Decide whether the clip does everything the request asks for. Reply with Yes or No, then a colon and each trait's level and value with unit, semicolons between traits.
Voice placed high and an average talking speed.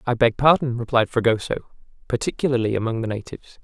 No: low, 120 Hz; average, 150 wpm